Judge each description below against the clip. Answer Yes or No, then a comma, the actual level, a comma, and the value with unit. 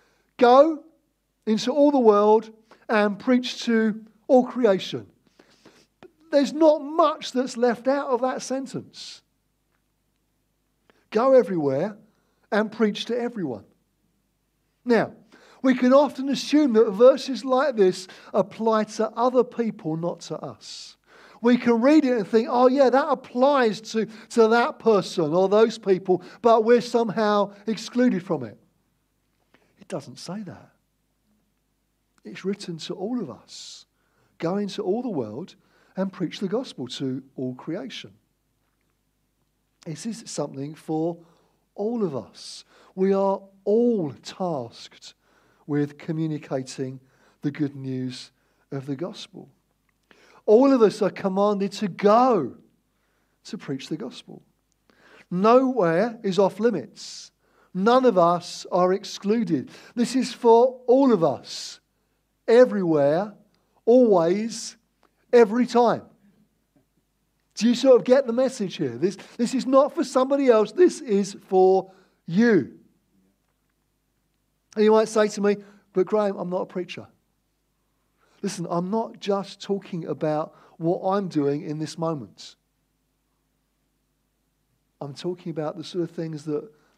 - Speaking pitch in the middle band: No, high, 210 Hz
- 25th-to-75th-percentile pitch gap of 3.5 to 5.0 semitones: No, wide, 5.6 semitones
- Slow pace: Yes, slow, 130 wpm